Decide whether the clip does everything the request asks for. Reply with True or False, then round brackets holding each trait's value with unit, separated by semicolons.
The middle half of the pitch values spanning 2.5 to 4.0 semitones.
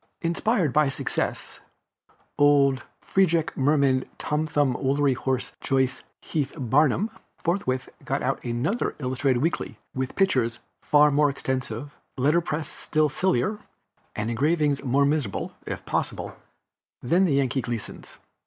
True (3.0 semitones)